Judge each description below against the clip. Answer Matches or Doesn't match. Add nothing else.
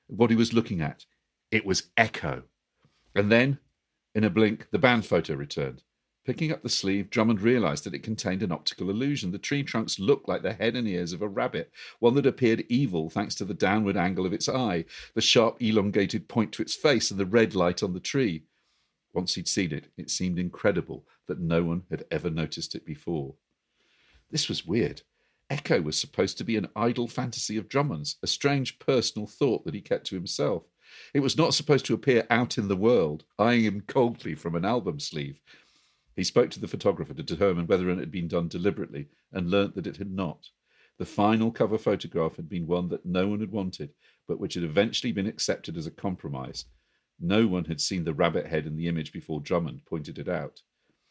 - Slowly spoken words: Doesn't match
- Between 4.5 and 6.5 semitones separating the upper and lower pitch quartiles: Matches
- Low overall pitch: Matches